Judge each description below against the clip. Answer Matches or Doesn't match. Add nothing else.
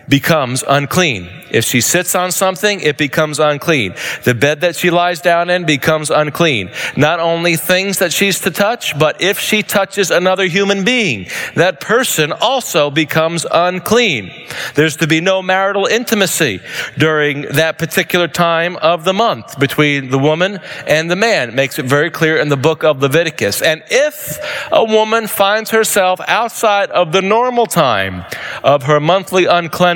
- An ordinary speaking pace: Matches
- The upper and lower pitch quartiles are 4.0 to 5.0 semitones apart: Matches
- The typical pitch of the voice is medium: Matches